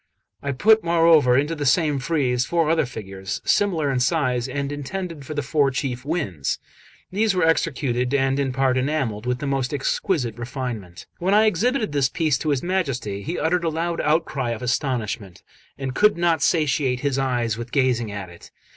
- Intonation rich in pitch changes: No, average, 4.6 semitones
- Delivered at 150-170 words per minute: No, average, 185 wpm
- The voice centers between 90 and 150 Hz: Yes, medium, 140 Hz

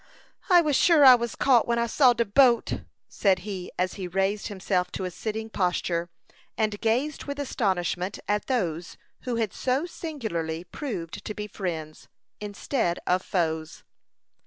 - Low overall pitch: No, high, 210 Hz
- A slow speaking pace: No, average, 160 wpm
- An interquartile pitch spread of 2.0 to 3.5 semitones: No, average, 5.2 semitones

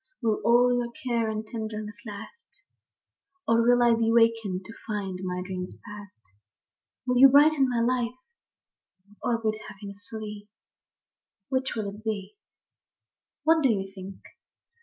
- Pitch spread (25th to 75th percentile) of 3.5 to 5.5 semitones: No, average, 3.0 semitones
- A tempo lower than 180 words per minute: Yes, average, 145 wpm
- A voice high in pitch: Yes, high, 225 Hz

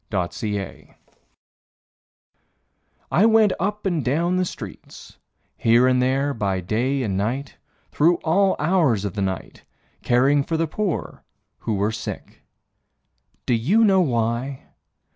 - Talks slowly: Yes, slow, 130 wpm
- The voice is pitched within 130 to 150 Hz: Yes, low, 135 Hz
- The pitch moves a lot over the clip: Yes, wide, 7.5 semitones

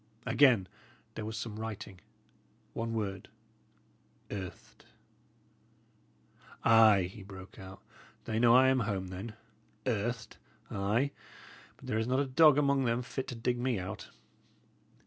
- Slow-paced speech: Yes, slow, 130 wpm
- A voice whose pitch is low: Yes, low, 110 Hz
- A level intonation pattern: No, average, 4.0 semitones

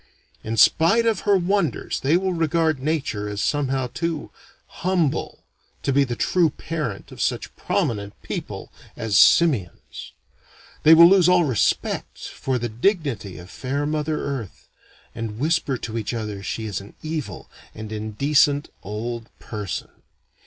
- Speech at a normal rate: Yes, average, 145 wpm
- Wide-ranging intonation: Yes, wide, 6.9 semitones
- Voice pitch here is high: No, low, 135 Hz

